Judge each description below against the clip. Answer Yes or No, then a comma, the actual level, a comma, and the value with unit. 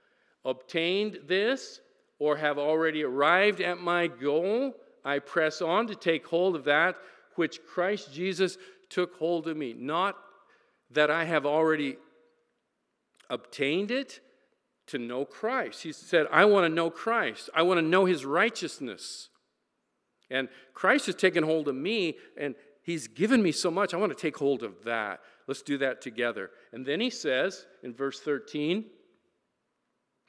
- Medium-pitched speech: Yes, medium, 165 Hz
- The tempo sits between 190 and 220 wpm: No, average, 155 wpm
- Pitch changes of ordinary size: Yes, average, 4.5 semitones